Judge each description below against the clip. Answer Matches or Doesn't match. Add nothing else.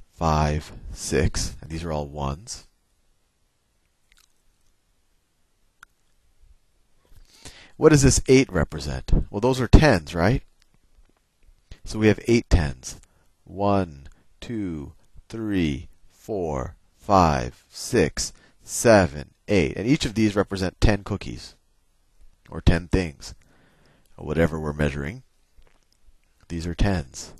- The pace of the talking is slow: Matches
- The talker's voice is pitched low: Matches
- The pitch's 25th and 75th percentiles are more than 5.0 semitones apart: Matches